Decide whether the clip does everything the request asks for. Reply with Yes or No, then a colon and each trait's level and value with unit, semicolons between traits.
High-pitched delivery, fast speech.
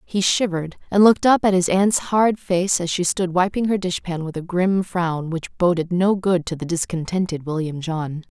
No: medium, 180 Hz; fast, 215 wpm